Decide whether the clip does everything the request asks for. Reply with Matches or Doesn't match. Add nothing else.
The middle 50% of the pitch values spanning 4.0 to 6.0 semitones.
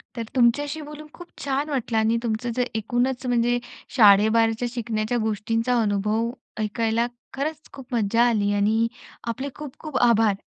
Doesn't match